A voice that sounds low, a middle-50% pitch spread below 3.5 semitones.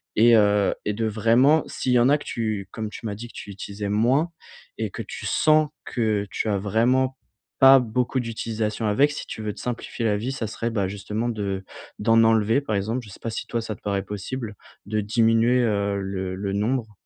Yes: low, 110 Hz; average, 2.7 semitones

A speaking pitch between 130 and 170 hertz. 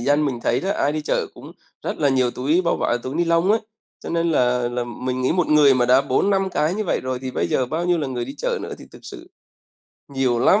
Yes: medium, 140 Hz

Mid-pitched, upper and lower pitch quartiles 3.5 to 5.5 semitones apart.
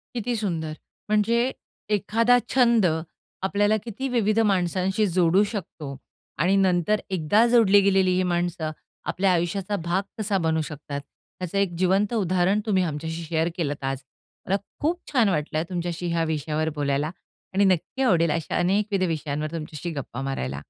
Yes: medium, 180 Hz; average, 4.3 semitones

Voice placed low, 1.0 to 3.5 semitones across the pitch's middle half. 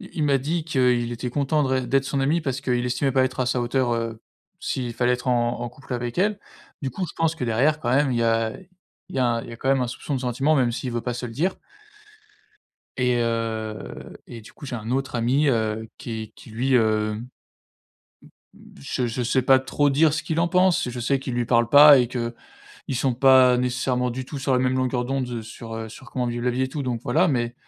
Yes: low, 125 Hz; narrow, 2.4 semitones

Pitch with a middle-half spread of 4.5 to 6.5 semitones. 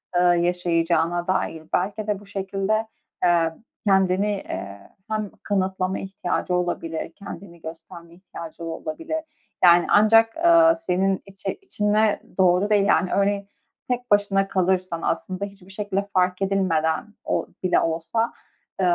No: average, 2.8 semitones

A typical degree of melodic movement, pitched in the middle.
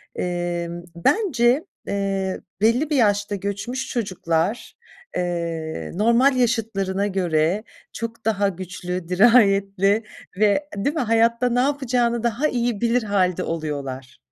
No: average, 4.7 semitones; high, 205 Hz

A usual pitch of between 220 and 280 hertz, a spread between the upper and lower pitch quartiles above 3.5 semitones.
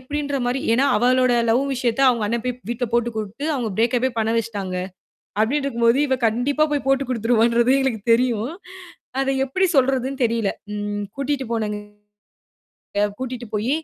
No: high, 240 Hz; average, 2.9 semitones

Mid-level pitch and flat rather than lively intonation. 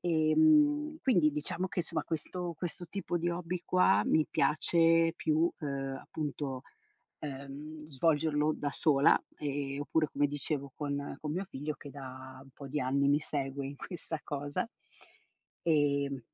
No: medium, 150 Hz; average, 3.0 semitones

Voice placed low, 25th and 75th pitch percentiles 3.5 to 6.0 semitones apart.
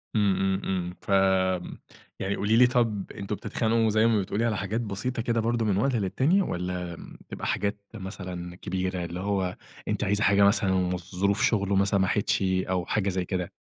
No: low, 100 Hz; average, 2.8 semitones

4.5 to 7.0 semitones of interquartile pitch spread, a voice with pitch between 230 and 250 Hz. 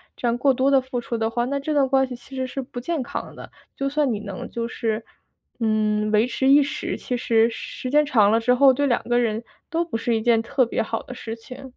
No: average, 3.1 semitones; high, 245 Hz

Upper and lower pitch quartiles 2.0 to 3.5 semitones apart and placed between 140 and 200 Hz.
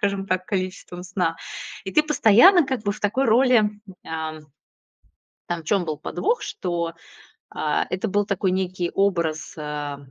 No: average, 3.9 semitones; medium, 185 Hz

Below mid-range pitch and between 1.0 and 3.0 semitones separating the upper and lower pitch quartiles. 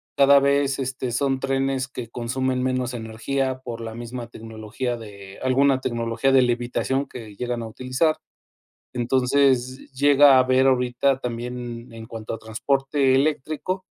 Yes: low, 130 Hz; narrow, 2.4 semitones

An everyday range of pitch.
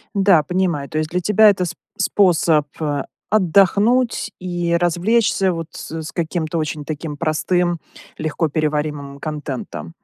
Yes: average, 3.2 semitones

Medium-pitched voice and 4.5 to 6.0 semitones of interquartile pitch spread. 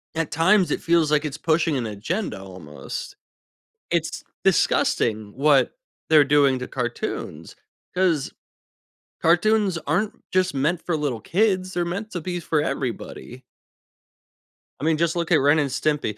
Yes: medium, 155 Hz; average, 4.8 semitones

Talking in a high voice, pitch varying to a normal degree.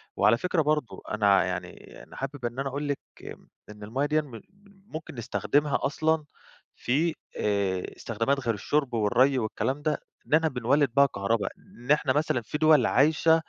No: low, 135 Hz; average, 4.5 semitones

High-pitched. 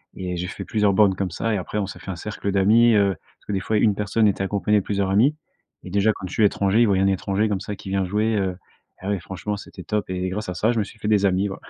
No: low, 100 Hz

